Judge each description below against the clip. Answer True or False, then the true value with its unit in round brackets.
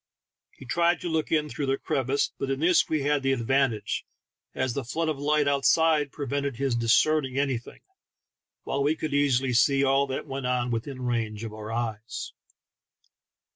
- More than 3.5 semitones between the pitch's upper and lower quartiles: False (3.0 semitones)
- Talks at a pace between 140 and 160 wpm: False (175 wpm)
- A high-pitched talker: False (135 Hz)